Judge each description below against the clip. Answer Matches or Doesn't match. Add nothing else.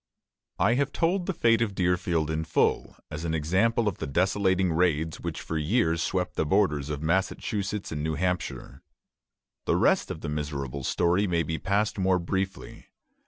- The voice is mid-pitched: Doesn't match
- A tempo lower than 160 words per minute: Doesn't match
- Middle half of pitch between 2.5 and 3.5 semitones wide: Doesn't match